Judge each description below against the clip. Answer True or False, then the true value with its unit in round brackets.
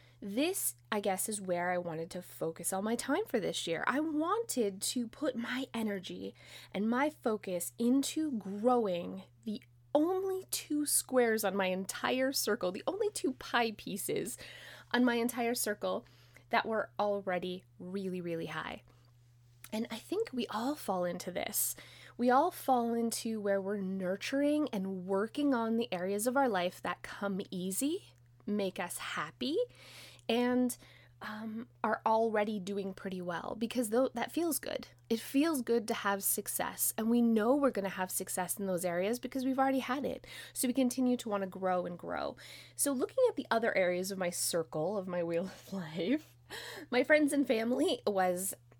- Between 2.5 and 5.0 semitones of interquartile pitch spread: False (5.6 semitones)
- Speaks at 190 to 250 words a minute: False (170 wpm)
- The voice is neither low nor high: False (220 Hz)